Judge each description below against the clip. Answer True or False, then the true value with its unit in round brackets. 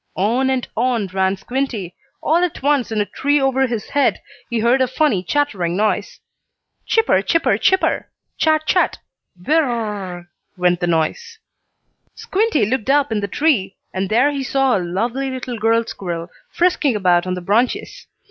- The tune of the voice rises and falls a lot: True (6.5 semitones)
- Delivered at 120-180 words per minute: True (175 wpm)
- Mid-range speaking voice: False (235 Hz)